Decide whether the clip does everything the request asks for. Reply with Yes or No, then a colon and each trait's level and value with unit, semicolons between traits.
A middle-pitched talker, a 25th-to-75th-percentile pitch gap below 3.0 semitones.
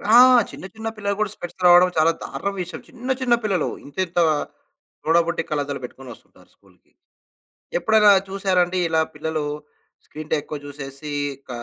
No: medium, 175 Hz; average, 4.7 semitones